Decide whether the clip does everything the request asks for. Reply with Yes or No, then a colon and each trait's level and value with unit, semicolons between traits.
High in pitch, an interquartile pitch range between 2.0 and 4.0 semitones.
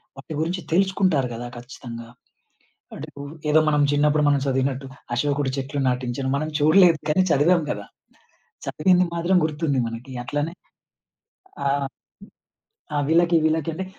No: medium, 145 Hz; average, 3.7 semitones